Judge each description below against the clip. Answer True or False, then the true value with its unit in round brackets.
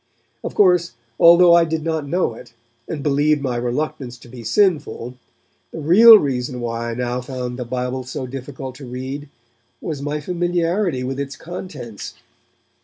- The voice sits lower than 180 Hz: True (140 Hz)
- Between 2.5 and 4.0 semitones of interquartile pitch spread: False (4.8 semitones)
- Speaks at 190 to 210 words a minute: False (160 wpm)